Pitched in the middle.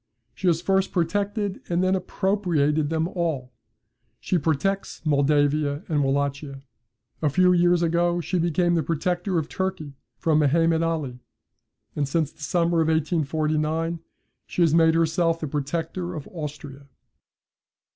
Yes: medium, 165 Hz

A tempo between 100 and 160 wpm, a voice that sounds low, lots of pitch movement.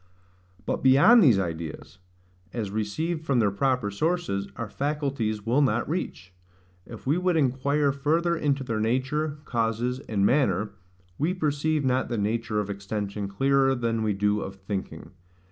Yes: average, 150 wpm; low, 125 Hz; wide, 5.7 semitones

